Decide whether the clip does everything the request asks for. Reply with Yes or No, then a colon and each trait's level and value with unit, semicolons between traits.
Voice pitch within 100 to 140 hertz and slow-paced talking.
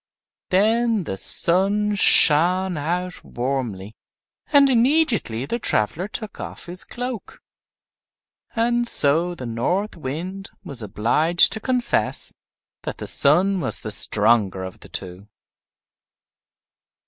No: medium, 175 Hz; slow, 110 wpm